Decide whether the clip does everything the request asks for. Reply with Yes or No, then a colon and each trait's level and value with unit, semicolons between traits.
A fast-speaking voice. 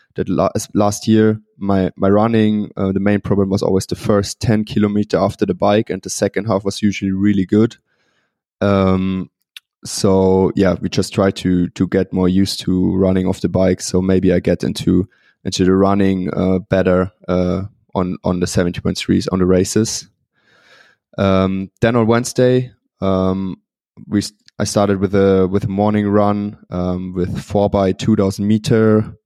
No: average, 170 wpm